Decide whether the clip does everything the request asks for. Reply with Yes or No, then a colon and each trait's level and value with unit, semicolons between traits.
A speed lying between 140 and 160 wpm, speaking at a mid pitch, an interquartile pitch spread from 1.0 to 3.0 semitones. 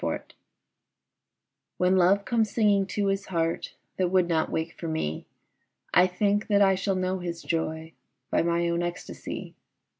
Yes: average, 155 wpm; medium, 180 Hz; average, 2.7 semitones